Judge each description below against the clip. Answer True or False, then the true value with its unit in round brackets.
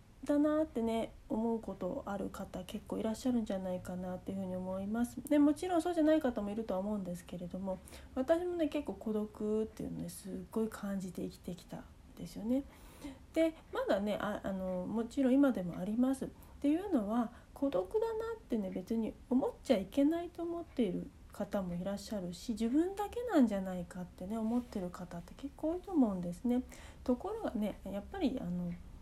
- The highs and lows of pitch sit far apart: True (6.7 semitones)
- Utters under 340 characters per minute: False (405 characters per minute)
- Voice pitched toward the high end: True (225 Hz)